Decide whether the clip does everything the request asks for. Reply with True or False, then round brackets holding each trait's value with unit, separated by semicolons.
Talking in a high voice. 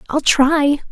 True (290 Hz)